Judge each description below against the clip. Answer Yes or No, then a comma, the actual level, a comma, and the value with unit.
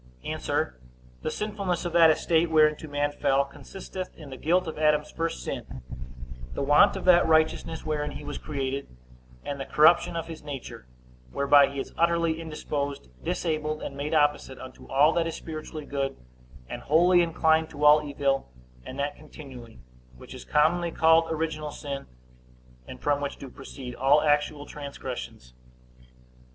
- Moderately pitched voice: Yes, medium, 150 Hz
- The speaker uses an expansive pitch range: No, narrow, 2.5 semitones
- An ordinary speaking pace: Yes, average, 160 wpm